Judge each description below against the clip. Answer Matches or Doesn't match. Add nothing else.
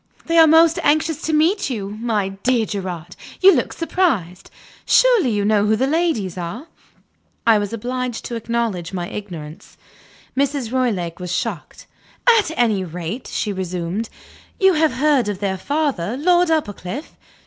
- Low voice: Doesn't match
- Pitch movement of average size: Doesn't match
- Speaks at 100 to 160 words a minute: Matches